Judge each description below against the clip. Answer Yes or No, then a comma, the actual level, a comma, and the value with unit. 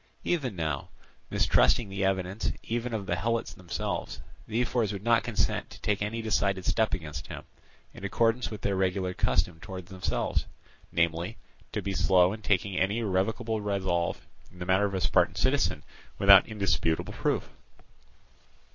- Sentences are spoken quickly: No, average, 155 wpm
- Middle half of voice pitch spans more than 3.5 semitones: No, average, 3.2 semitones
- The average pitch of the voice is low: Yes, low, 100 Hz